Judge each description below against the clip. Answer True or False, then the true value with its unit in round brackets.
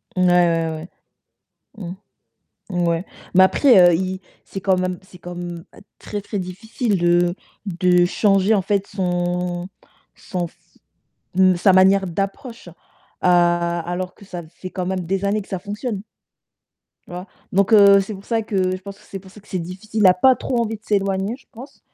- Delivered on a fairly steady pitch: True (2.1 semitones)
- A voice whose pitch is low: False (185 Hz)